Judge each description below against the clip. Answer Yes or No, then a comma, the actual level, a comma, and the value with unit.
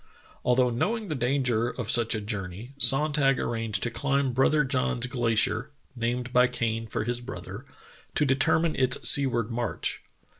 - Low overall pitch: Yes, low, 125 Hz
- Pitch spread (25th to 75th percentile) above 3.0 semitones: No, average, 2.7 semitones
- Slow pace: No, average, 155 wpm